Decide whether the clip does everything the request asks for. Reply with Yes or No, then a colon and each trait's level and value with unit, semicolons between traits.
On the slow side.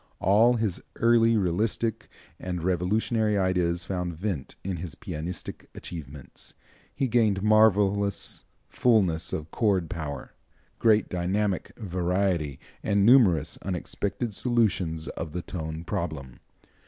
Yes: slow, 110 wpm